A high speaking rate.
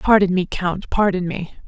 No: average, 180 wpm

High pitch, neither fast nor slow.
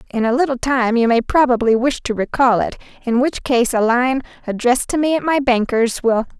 No: very high, 250 Hz; fast, 215 wpm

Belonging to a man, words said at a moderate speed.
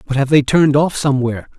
No: male; fast, 230 wpm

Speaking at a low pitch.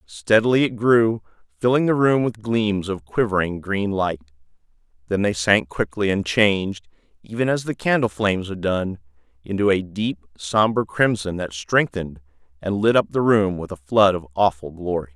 Yes: low, 100 Hz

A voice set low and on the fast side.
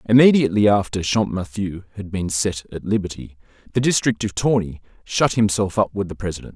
No: low, 100 Hz; average, 155 wpm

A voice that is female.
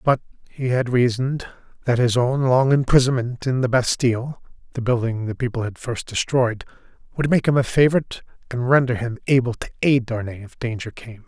No: male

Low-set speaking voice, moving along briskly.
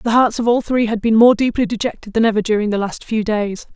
No: high, 220 Hz; fast, 270 wpm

